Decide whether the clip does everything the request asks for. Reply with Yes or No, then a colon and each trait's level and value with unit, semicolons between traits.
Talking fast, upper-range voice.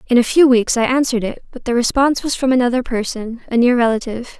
Yes: fast, 230 wpm; high, 245 Hz